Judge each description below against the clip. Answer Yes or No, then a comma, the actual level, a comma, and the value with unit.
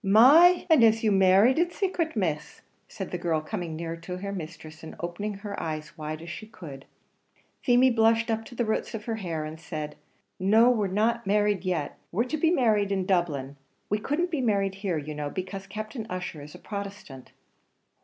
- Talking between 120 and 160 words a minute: No, average, 200 wpm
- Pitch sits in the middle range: No, high, 195 Hz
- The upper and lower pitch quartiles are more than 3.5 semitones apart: Yes, average, 5.2 semitones